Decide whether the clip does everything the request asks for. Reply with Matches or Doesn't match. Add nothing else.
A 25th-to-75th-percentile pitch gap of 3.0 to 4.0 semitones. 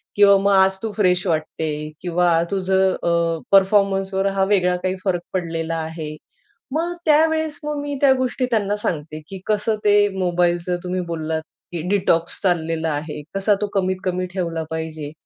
Matches